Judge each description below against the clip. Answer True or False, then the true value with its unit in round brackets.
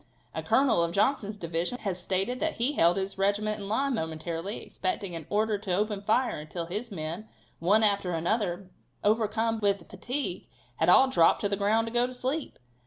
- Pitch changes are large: False (4.2 semitones)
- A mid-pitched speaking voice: False (205 Hz)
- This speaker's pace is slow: False (185 wpm)